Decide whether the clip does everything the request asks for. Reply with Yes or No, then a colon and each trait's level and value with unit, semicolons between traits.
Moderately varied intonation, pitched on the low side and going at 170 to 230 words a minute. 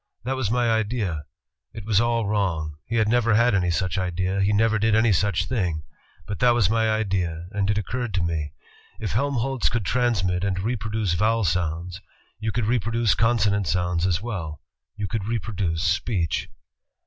Yes: average, 4.1 semitones; low, 105 Hz; average, 175 wpm